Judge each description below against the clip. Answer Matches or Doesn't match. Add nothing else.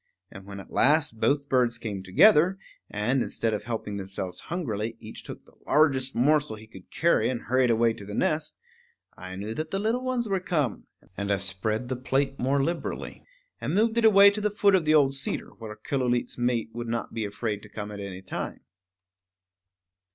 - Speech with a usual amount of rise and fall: Doesn't match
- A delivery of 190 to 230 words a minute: Matches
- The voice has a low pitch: Matches